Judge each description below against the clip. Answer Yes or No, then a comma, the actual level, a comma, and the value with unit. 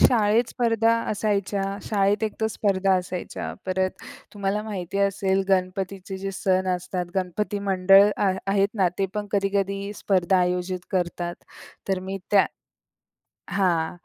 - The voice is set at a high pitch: Yes, high, 195 Hz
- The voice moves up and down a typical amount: No, narrow, 1.5 semitones